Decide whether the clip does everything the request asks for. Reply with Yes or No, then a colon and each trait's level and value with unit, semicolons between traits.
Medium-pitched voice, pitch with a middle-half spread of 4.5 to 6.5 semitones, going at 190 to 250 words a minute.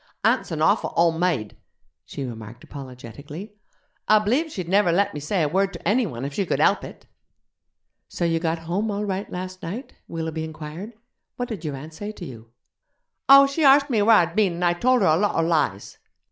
Yes: medium, 175 Hz; average, 5.0 semitones; average, 200 wpm